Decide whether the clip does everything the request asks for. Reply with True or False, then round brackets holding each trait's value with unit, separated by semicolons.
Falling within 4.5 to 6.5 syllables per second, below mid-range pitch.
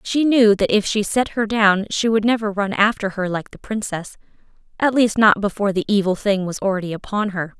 False (5.4 syllables/s; 205 Hz)